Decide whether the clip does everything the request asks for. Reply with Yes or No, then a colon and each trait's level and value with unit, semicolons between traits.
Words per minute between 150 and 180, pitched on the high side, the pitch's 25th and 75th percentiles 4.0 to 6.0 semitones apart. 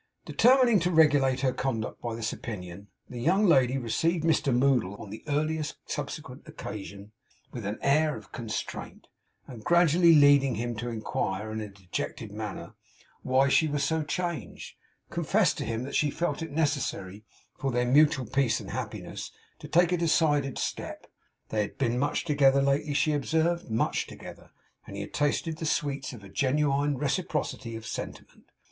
No: average, 165 wpm; medium, 140 Hz; average, 5.0 semitones